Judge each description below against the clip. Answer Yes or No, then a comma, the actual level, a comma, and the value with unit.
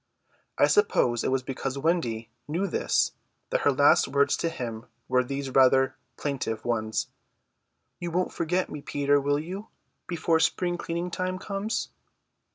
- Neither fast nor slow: Yes, average, 150 wpm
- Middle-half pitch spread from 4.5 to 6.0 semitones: Yes, average, 5.0 semitones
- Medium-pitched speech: Yes, medium, 145 Hz